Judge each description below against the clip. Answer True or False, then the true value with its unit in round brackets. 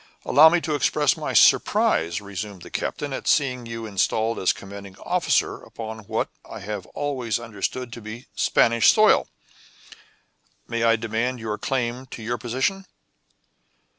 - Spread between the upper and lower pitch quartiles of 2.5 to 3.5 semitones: True (3.2 semitones)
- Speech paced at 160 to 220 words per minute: False (145 wpm)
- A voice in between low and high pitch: False (115 Hz)